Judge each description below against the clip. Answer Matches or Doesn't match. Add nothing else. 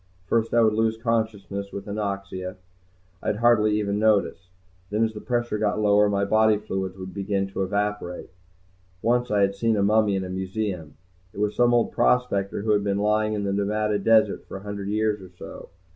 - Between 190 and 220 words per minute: Matches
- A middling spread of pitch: Doesn't match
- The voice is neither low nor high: Doesn't match